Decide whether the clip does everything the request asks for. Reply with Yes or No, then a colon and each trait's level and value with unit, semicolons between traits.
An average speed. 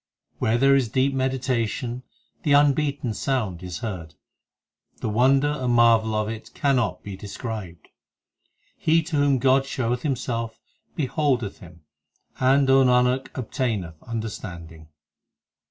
No: slow, 120 wpm